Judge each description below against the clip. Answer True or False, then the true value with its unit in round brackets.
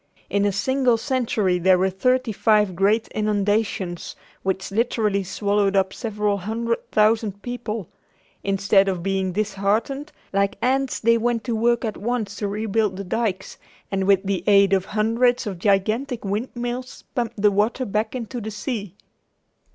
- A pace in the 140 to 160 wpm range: True (150 wpm)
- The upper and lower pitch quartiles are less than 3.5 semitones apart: True (2.9 semitones)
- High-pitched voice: True (210 Hz)